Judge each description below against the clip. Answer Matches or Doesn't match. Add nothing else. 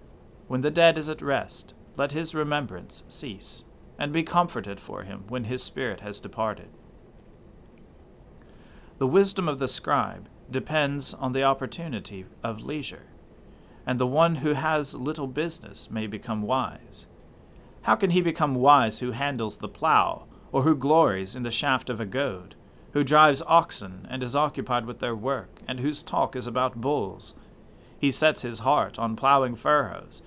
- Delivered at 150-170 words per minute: Matches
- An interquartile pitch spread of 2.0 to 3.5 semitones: Doesn't match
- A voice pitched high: Doesn't match